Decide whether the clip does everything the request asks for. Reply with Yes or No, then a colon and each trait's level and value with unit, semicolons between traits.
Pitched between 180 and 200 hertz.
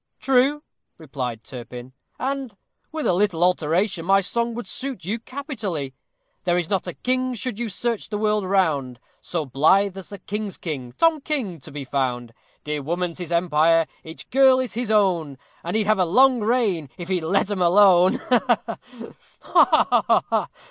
Yes: high, 190 Hz